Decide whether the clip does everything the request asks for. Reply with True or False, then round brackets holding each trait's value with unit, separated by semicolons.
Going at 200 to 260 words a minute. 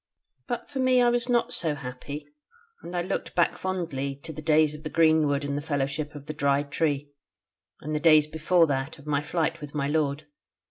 True (205 wpm)